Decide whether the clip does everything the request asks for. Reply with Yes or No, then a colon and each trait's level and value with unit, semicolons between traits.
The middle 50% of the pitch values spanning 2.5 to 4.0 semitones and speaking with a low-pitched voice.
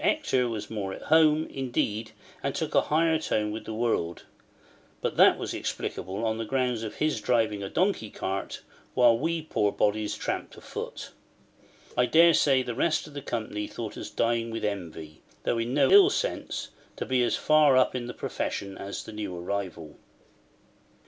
No: average, 4.7 semitones; low, 115 Hz